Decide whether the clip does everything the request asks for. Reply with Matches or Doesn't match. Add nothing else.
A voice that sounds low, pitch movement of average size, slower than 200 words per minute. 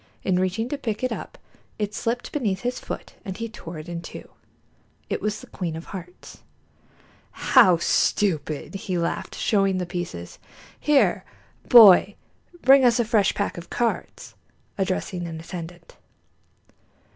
Doesn't match